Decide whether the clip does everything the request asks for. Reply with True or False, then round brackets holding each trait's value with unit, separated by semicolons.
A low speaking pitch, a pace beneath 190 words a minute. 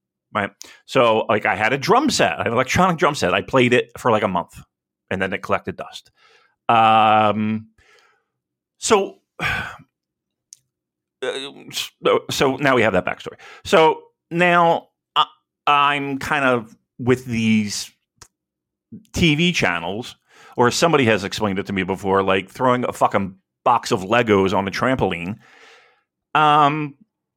True (115 Hz; 135 wpm)